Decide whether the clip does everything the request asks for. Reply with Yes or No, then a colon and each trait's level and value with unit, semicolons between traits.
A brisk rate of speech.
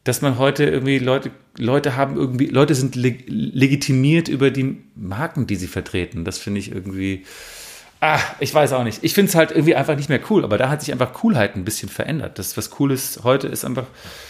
Yes: fast, 220 wpm